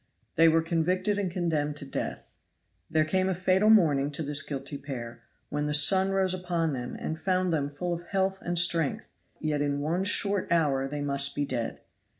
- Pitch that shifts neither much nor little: Yes, average, 4.3 semitones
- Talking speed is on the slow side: No, average, 190 wpm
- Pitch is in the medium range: Yes, medium, 160 Hz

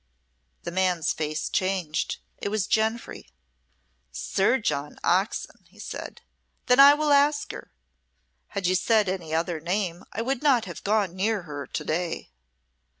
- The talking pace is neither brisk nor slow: Yes, average, 150 wpm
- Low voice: No, high, 190 Hz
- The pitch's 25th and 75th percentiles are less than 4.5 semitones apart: No, average, 4.8 semitones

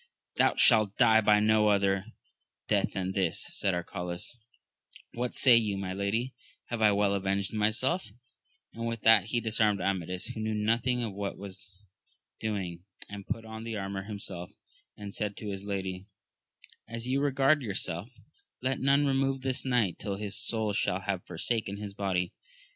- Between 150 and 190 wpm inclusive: Yes, average, 165 wpm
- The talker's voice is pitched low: Yes, low, 105 Hz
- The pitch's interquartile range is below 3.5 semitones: Yes, average, 2.9 semitones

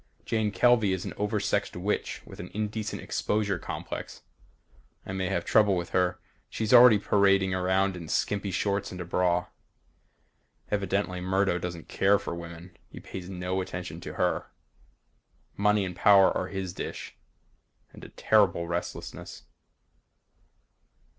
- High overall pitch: No, very low, 95 Hz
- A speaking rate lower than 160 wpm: Yes, average, 140 wpm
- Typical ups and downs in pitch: No, narrow, 2.3 semitones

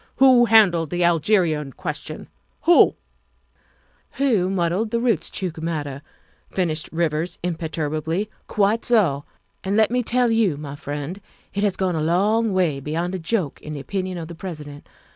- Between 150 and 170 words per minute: Yes, average, 160 wpm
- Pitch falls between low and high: Yes, medium, 175 Hz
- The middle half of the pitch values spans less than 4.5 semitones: No, average, 5.1 semitones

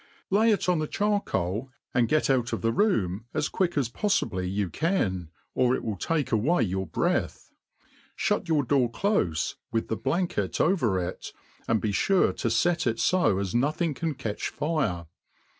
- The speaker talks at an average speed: Yes, average, 175 wpm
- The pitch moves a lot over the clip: Yes, wide, 8.5 semitones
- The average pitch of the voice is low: Yes, low, 125 Hz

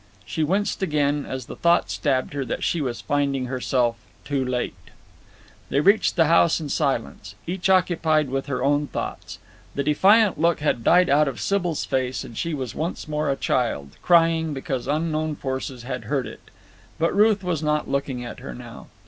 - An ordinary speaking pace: Yes, average, 180 wpm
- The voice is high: No, medium, 145 Hz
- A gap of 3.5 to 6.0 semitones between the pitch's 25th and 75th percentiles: Yes, average, 4.1 semitones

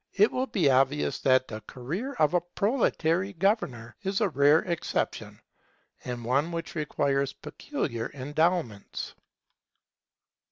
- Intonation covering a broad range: Yes, wide, 6.3 semitones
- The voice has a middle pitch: Yes, medium, 155 Hz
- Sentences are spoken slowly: Yes, slow, 120 wpm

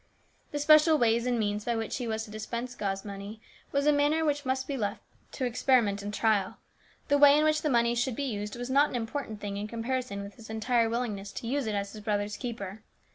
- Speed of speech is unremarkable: No, fast, 235 wpm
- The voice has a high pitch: Yes, high, 235 Hz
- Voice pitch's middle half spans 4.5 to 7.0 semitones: No, average, 4.1 semitones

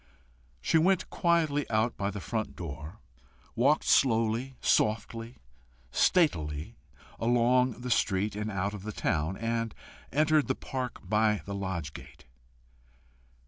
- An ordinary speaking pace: No, slow, 125 wpm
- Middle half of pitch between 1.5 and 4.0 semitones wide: No, average, 4.4 semitones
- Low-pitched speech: Yes, low, 115 Hz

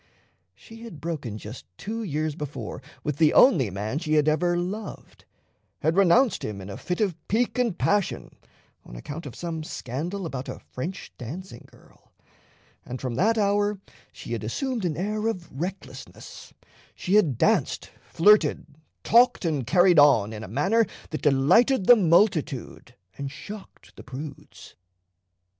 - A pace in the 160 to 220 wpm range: No, average, 150 wpm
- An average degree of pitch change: No, wide, 6.8 semitones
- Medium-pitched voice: Yes, medium, 165 Hz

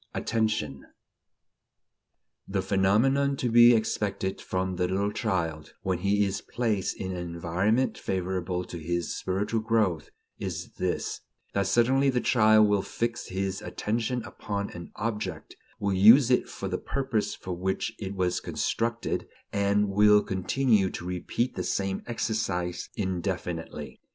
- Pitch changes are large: No, average, 3.4 semitones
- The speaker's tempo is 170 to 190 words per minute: No, average, 140 wpm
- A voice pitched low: Yes, low, 100 Hz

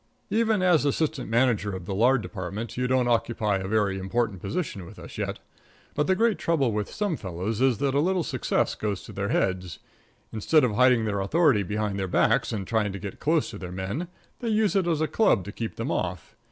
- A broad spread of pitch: Yes, wide, 7.5 semitones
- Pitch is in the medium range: No, low, 115 Hz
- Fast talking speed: Yes, fast, 220 wpm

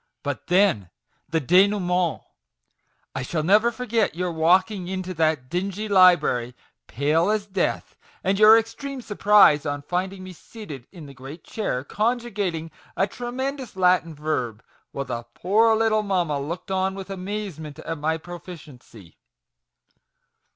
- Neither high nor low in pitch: Yes, medium, 180 Hz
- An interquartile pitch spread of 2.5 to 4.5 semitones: No, average, 5.1 semitones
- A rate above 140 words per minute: No, slow, 135 wpm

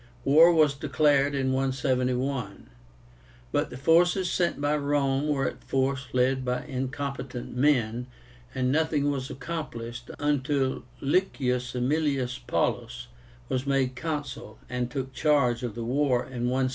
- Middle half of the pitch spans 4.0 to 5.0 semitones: No, narrow, 2.5 semitones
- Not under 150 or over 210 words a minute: No, slow, 135 wpm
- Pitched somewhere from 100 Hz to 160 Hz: Yes, low, 135 Hz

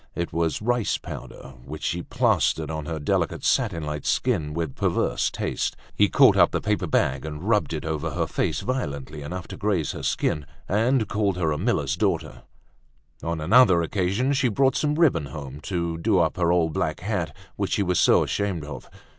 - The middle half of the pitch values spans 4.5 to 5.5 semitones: Yes, average, 5.2 semitones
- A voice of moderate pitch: No, very low, 85 Hz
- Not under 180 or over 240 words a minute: Yes, average, 190 wpm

